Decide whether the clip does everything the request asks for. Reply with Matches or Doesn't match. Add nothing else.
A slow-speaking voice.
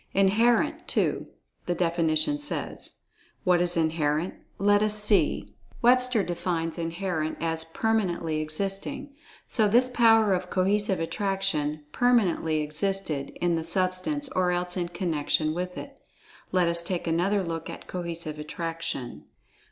Matches